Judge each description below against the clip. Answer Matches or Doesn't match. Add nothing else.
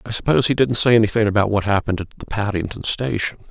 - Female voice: Doesn't match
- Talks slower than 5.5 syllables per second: Doesn't match